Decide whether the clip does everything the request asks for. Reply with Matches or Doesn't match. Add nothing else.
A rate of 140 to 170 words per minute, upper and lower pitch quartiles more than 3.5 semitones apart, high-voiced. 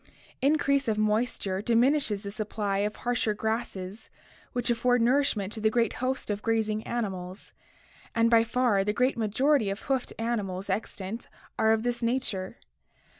Doesn't match